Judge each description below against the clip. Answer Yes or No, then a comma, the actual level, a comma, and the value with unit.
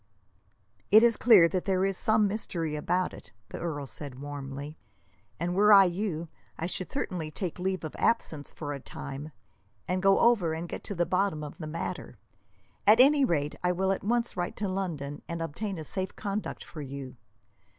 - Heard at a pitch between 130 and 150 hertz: No, medium, 180 Hz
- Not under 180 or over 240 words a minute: Yes, average, 190 wpm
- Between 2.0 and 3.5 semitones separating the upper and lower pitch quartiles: No, average, 4.5 semitones